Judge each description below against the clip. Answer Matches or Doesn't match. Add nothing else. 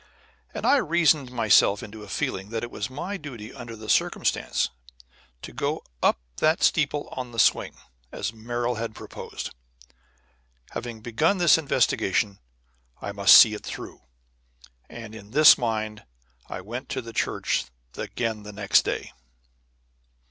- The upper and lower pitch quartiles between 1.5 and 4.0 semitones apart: Matches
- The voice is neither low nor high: Doesn't match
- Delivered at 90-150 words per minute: Matches